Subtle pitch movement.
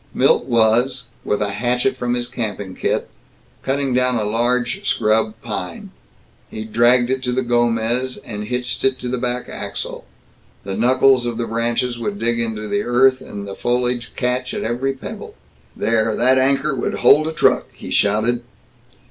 Yes: narrow, 2.2 semitones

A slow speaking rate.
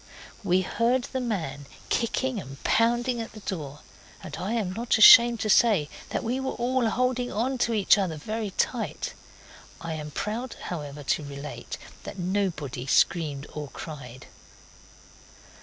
No: average, 150 wpm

